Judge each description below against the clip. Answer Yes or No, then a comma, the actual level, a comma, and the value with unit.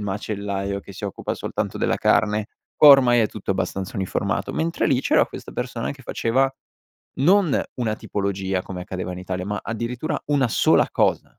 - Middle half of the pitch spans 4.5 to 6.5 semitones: Yes, average, 4.8 semitones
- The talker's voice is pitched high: No, low, 105 Hz